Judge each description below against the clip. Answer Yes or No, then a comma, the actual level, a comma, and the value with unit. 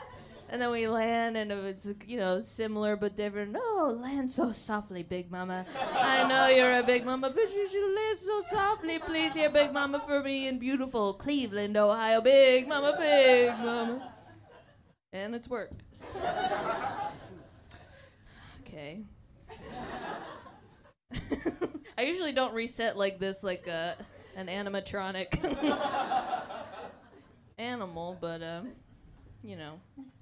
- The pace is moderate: No, slow, 125 wpm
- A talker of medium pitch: No, high, 245 Hz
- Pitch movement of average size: No, wide, 6.0 semitones